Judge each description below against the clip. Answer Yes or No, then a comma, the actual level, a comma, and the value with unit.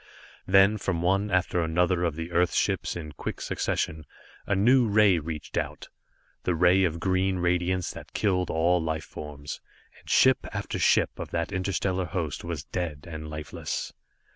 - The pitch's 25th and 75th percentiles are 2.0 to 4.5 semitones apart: Yes, average, 2.8 semitones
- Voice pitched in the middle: No, very low, 90 Hz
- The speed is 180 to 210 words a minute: No, average, 165 wpm